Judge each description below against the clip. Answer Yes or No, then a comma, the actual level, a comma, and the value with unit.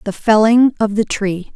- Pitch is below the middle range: No, high, 215 Hz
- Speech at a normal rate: Yes, average, 195 wpm